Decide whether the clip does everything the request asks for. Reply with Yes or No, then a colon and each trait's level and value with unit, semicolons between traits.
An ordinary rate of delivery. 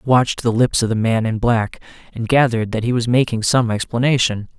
No: fast, 225 wpm